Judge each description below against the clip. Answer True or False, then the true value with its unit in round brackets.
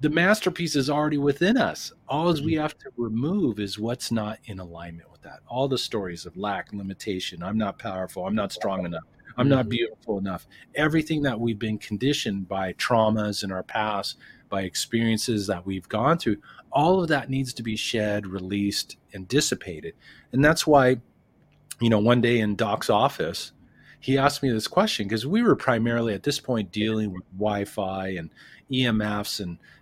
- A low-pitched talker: True (115 Hz)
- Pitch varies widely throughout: True (5.7 semitones)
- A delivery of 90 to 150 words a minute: False (180 wpm)